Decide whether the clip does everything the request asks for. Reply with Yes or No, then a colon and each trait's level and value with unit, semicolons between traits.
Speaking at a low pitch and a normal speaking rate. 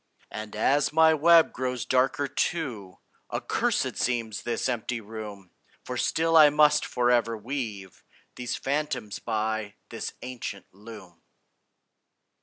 No: low, 120 Hz; slow, 115 wpm